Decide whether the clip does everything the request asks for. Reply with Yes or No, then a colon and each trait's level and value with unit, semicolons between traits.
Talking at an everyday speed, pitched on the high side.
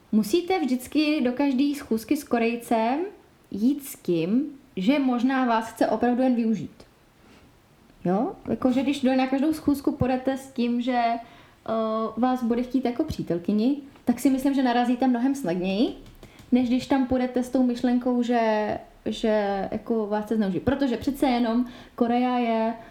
Yes: average, 150 wpm; very high, 250 Hz